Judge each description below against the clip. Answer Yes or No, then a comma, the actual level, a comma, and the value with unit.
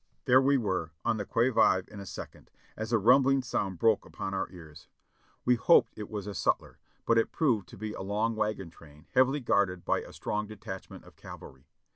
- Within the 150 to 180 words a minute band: No, fast, 205 wpm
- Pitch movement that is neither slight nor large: Yes, average, 3.7 semitones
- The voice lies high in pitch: No, low, 105 Hz